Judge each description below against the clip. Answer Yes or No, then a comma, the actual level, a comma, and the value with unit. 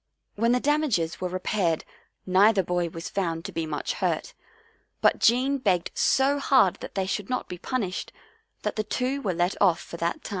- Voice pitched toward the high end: Yes, high, 195 Hz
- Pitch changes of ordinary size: No, wide, 6.2 semitones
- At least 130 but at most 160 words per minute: No, average, 190 wpm